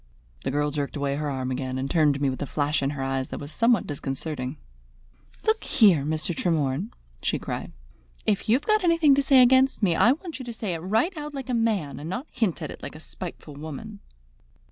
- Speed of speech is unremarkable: No, fast, 230 wpm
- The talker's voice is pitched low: No, medium, 165 Hz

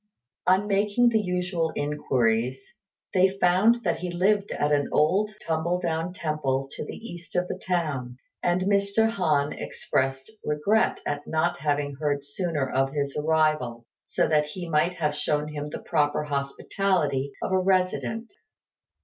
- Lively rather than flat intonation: No, average, 4.2 semitones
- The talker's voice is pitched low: No, medium, 160 Hz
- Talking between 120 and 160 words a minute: Yes, average, 150 wpm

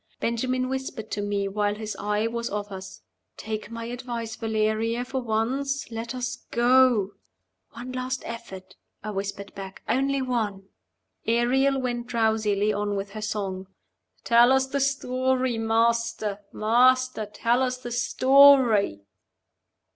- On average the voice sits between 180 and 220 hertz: No, high, 230 Hz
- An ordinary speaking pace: No, slow, 130 wpm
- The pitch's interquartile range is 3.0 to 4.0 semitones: Yes, average, 3.3 semitones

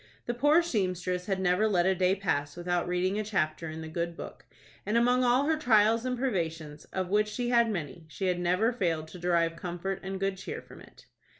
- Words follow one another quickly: Yes, fast, 210 wpm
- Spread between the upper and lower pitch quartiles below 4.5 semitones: Yes, average, 4.1 semitones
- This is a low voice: No, high, 190 Hz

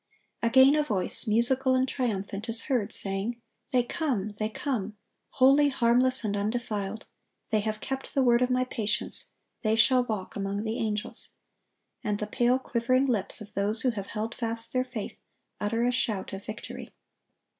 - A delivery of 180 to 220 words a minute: No, average, 170 wpm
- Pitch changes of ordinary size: Yes, average, 3.2 semitones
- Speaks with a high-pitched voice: Yes, high, 230 Hz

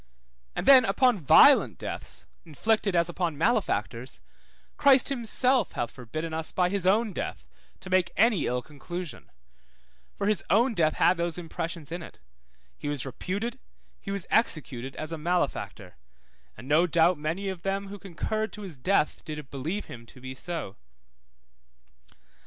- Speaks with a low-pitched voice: No, medium, 175 Hz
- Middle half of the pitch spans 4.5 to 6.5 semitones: Yes, average, 4.9 semitones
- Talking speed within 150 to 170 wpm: Yes, average, 155 wpm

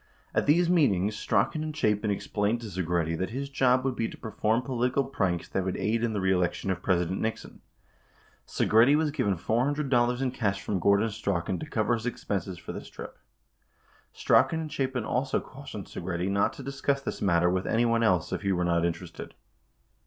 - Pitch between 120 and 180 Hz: No, low, 110 Hz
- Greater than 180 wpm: Yes, average, 190 wpm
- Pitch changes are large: Yes, wide, 5.7 semitones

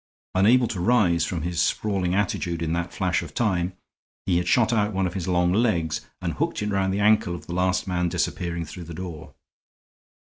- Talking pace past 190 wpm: Yes, average, 200 wpm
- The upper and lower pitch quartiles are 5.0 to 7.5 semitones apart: No, average, 2.9 semitones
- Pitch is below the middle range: Yes, very low, 90 Hz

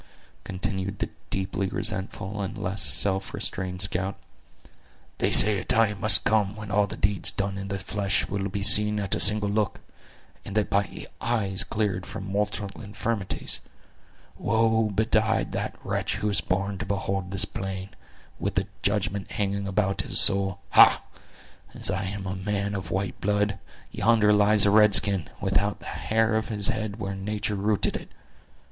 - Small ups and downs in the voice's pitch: Yes, narrow, 1.5 semitones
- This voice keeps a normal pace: Yes, average, 165 wpm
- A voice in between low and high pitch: No, low, 100 Hz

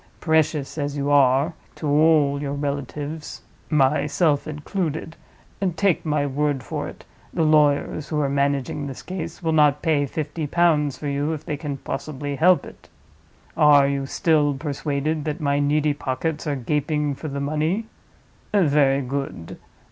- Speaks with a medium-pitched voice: Yes, medium, 145 Hz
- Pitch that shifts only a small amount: Yes, narrow, 1.7 semitones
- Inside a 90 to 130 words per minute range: No, average, 150 wpm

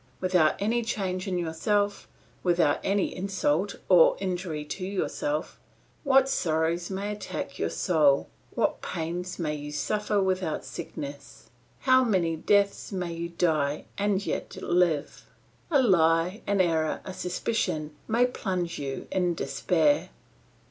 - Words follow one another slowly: Yes, slow, 130 wpm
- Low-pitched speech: No, medium, 180 Hz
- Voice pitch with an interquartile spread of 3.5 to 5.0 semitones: Yes, average, 3.9 semitones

